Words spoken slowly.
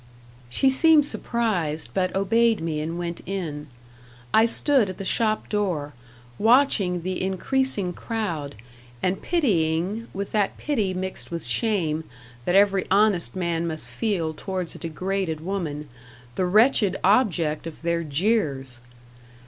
Yes: slow, 130 wpm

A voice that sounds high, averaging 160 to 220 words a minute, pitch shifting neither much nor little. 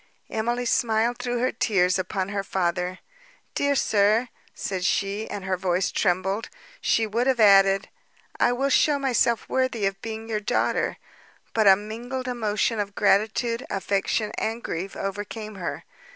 No: high, 215 Hz; average, 150 wpm; average, 3.4 semitones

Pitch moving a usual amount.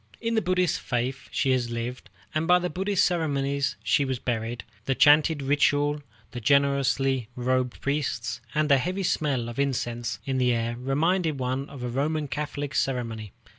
Yes: average, 3.5 semitones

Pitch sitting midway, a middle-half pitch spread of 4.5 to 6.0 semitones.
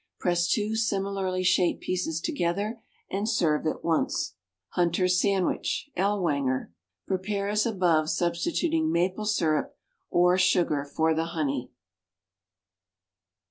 No: medium, 180 Hz; average, 3.5 semitones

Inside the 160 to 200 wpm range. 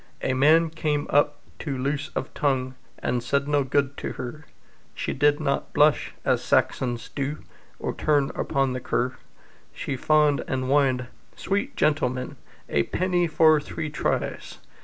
No: average, 150 wpm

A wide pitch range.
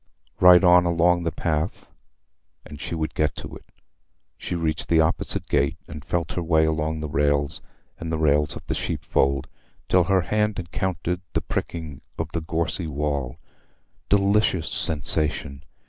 No: average, 2.7 semitones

